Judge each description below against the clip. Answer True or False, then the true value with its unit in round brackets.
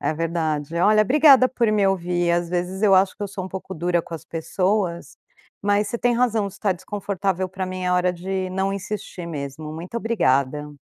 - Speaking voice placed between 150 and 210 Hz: True (185 Hz)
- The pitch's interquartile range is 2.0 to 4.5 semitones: True (3.1 semitones)